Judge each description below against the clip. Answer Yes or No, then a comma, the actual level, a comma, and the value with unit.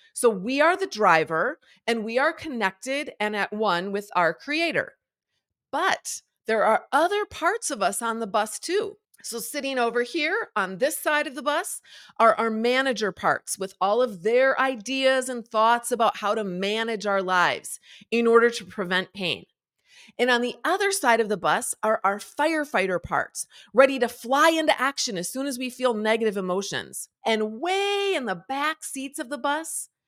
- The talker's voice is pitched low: No, high, 235 Hz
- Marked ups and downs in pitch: Yes, wide, 5.7 semitones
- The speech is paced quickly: No, average, 180 wpm